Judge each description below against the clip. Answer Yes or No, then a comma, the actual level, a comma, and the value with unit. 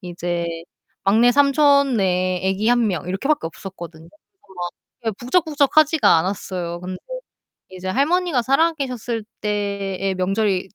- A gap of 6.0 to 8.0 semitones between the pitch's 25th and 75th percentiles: Yes, wide, 7.0 semitones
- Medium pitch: No, high, 200 Hz